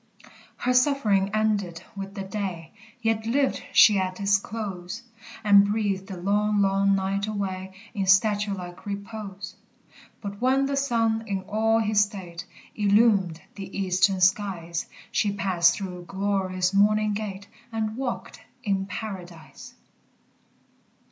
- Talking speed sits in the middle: No, slow, 130 wpm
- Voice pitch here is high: Yes, high, 200 Hz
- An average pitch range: No, narrow, 2.2 semitones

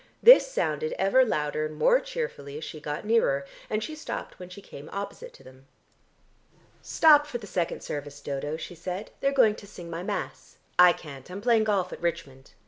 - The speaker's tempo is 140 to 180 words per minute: No, average, 195 wpm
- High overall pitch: No, medium, 180 Hz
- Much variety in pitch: Yes, wide, 7.9 semitones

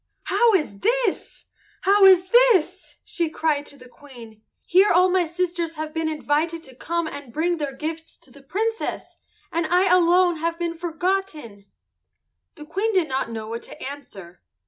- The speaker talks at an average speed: Yes, average, 170 wpm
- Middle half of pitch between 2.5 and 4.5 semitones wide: Yes, average, 4.2 semitones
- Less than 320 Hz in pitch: No, very high, 330 Hz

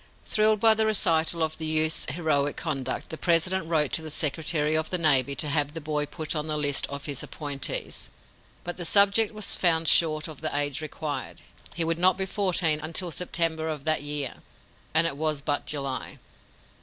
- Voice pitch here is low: No, medium, 160 Hz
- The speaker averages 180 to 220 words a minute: Yes, average, 195 wpm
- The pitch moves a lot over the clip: No, narrow, 2.4 semitones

